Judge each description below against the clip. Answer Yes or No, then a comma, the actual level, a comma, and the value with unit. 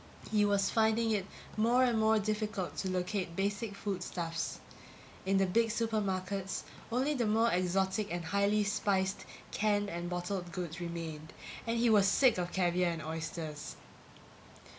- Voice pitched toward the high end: Yes, high, 195 Hz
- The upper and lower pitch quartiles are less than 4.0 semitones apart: Yes, average, 3.3 semitones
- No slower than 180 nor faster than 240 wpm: No, average, 150 wpm